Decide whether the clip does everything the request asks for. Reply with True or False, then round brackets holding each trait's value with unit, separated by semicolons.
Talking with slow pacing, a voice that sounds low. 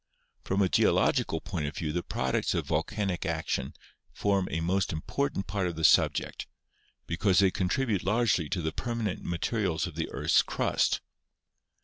False (155 wpm; 95 Hz)